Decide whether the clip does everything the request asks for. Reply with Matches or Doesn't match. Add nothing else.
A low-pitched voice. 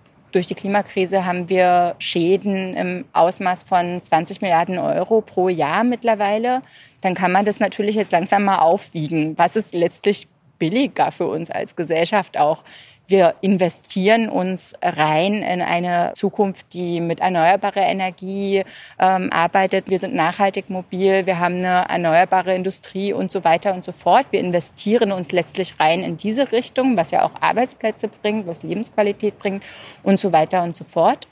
Doesn't match